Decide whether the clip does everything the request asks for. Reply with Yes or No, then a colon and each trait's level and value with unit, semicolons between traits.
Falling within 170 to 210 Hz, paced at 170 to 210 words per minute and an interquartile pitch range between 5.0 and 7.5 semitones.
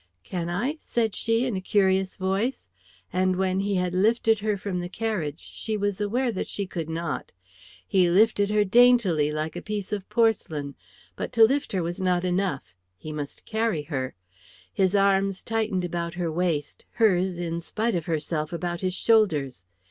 No: high, 190 Hz; average, 175 wpm; average, 3.9 semitones